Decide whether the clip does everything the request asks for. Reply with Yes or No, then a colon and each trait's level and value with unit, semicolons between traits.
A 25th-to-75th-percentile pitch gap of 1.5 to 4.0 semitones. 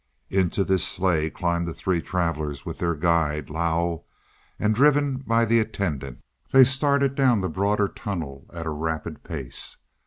No: average, 5.3 semitones